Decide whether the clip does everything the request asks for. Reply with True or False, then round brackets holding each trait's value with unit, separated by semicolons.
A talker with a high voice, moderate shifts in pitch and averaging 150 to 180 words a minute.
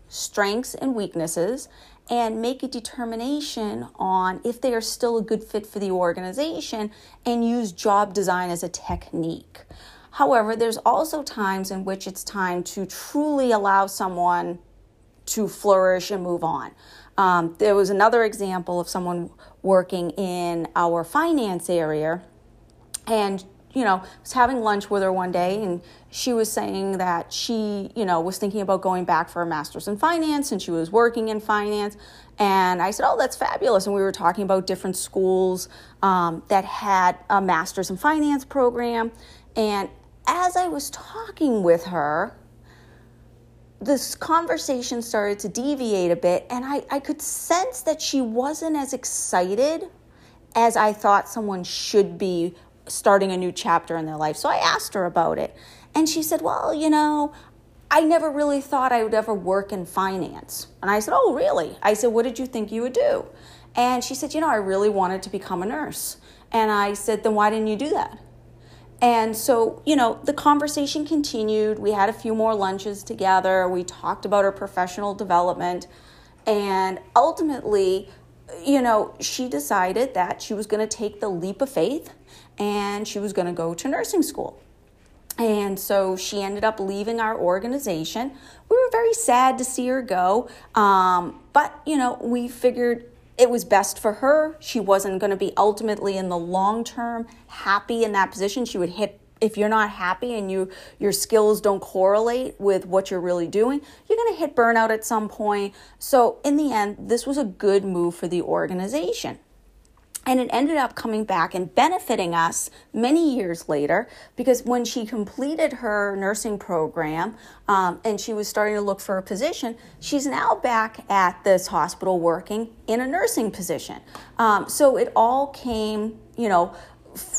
True (210 Hz; 4.6 semitones; 175 wpm)